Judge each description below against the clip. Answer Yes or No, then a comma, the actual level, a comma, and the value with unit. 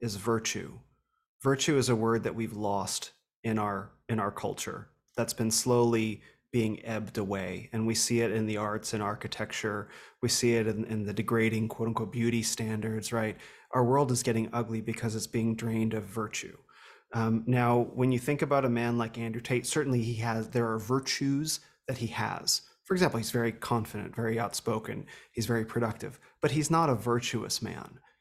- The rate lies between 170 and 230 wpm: Yes, average, 185 wpm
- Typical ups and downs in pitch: No, narrow, 1.6 semitones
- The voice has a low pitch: Yes, low, 115 Hz